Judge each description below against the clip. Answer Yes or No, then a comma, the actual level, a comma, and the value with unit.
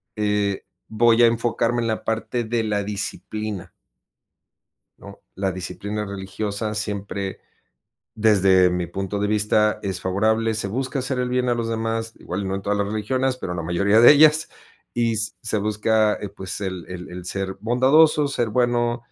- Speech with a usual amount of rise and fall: Yes, average, 3.0 semitones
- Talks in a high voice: No, low, 105 Hz